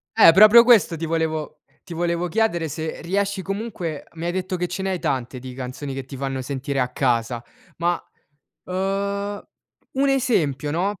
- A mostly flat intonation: No, wide, 5.9 semitones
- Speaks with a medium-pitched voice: Yes, medium, 170 Hz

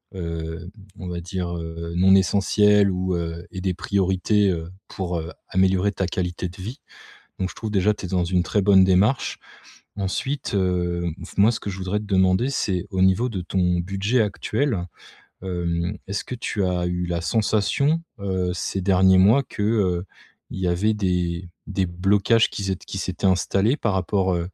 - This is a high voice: No, very low, 95 Hz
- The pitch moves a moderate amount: No, narrow, 2.3 semitones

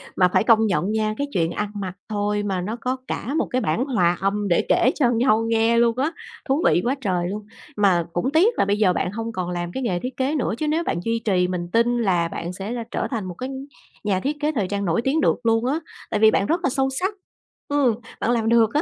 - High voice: Yes, high, 220 Hz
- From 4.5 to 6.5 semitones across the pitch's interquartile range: Yes, average, 5.1 semitones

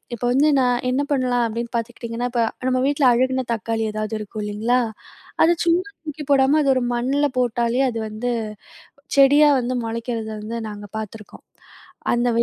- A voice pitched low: No, high, 245 Hz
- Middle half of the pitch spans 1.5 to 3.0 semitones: Yes, narrow, 2.6 semitones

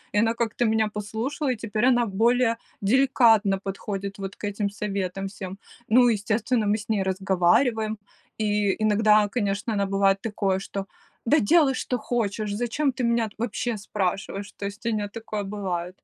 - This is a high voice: Yes, high, 210 Hz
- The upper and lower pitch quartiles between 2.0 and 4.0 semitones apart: Yes, average, 2.7 semitones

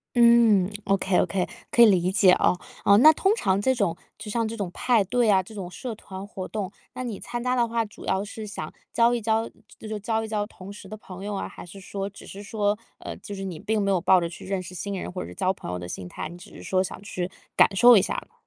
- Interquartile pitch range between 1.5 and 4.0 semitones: Yes, average, 3.0 semitones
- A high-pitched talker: Yes, high, 200 Hz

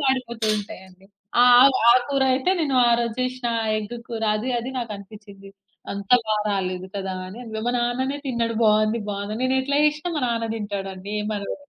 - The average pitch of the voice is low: No, high, 230 Hz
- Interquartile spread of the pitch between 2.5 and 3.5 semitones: No, average, 4.0 semitones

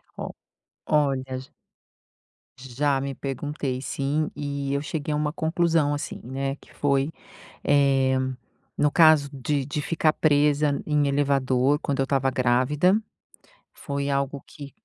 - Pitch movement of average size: No, narrow, 1.6 semitones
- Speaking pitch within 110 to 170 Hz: Yes, medium, 140 Hz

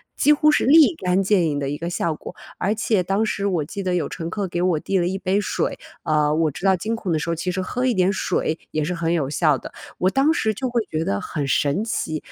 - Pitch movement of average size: Yes, average, 4.4 semitones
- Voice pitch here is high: No, medium, 180 Hz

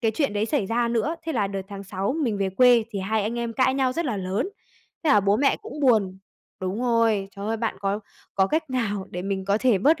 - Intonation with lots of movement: No, average, 4.3 semitones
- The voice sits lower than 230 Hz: Yes, high, 220 Hz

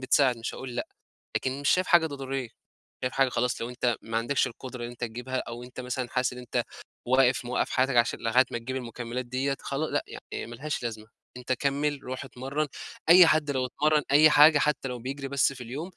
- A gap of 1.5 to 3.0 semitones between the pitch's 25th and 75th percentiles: Yes, narrow, 2.4 semitones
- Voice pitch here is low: Yes, low, 130 Hz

